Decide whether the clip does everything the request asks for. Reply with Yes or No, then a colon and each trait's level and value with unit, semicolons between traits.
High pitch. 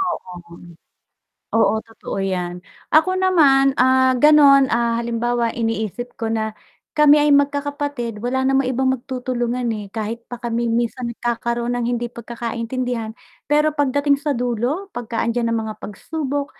Yes: high, 245 Hz